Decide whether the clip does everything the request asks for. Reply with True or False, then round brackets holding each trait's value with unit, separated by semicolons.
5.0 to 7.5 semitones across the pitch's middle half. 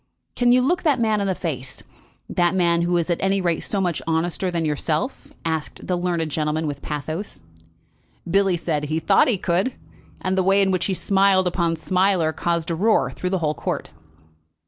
False (3.1 semitones)